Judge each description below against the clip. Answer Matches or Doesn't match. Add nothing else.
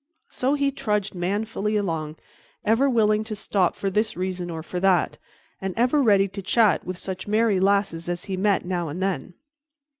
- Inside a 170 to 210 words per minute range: Matches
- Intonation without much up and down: Doesn't match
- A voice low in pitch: Doesn't match